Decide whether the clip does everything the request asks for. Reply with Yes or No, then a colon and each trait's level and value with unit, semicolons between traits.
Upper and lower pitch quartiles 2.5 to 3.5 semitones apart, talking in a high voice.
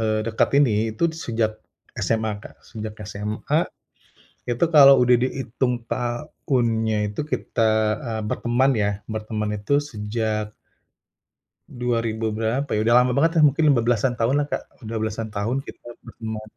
No: average, 2.9 semitones; low, 115 Hz